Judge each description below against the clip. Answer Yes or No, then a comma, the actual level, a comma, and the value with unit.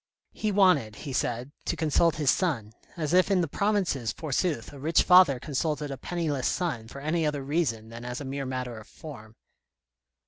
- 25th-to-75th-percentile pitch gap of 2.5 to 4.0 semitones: No, average, 5.3 semitones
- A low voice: No, medium, 145 Hz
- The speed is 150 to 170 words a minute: No, average, 185 wpm